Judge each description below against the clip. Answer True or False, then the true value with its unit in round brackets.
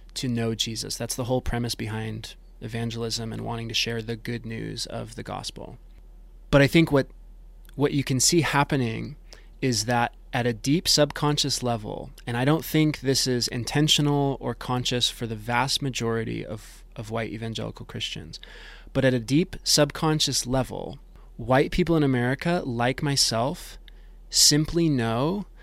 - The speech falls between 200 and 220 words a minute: False (155 wpm)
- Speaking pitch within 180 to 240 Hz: False (125 Hz)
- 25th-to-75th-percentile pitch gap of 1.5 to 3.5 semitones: False (3.9 semitones)